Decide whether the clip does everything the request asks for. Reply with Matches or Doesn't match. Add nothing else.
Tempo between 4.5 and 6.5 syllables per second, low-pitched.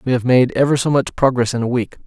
Doesn't match